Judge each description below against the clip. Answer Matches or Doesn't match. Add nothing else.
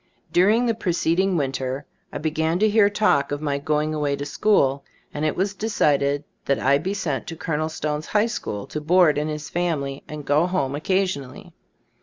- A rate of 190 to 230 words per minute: Matches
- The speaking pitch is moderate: Matches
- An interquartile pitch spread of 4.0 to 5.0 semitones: Matches